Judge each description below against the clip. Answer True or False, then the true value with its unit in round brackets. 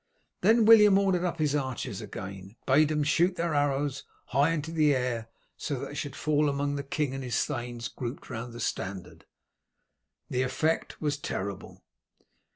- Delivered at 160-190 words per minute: True (165 wpm)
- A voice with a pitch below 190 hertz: True (140 Hz)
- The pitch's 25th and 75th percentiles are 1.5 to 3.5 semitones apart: False (4.2 semitones)